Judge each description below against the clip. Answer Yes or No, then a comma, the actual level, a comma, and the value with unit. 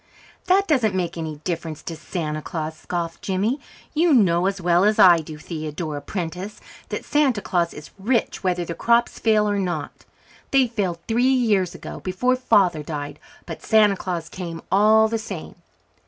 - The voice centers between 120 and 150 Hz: No, medium, 185 Hz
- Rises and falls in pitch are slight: No, average, 4.7 semitones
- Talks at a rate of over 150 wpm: Yes, average, 170 wpm